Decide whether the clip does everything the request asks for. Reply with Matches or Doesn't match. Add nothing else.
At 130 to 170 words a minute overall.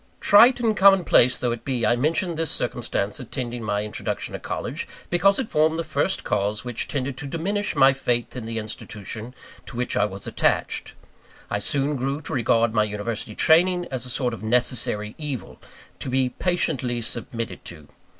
Doesn't match